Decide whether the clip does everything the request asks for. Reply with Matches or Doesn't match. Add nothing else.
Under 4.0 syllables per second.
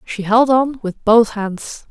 Matches